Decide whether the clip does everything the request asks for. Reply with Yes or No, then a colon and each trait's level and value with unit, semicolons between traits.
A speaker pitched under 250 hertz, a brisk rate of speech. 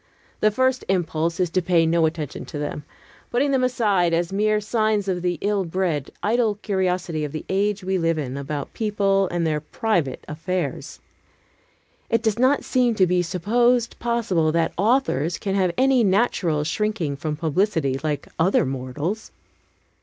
No: medium, 185 Hz; average, 160 wpm